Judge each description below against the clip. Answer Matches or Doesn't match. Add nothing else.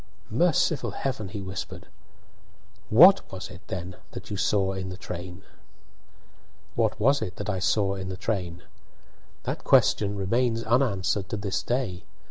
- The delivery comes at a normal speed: Matches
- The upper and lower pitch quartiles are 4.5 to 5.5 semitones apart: Doesn't match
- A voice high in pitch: Doesn't match